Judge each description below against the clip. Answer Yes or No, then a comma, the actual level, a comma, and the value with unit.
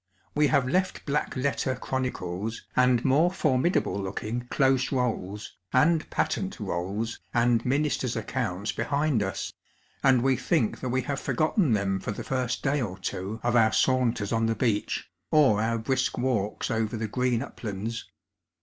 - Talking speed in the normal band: Yes, average, 160 wpm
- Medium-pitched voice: No, low, 120 Hz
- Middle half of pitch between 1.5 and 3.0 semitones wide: No, average, 3.5 semitones